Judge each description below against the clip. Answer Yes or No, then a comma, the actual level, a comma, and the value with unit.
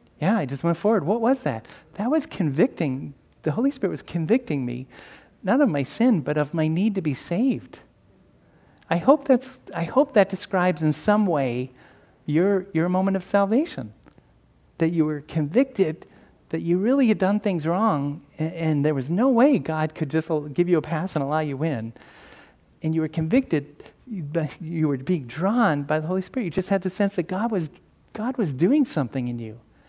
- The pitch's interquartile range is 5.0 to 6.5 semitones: Yes, wide, 5.5 semitones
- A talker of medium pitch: Yes, medium, 175 Hz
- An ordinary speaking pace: No, fast, 195 wpm